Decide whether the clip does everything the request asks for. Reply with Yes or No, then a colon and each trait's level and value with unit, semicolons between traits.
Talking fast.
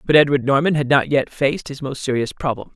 Yes: fast, 240 wpm